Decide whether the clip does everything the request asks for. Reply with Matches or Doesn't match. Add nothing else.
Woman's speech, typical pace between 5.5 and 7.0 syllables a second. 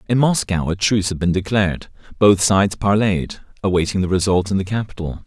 Doesn't match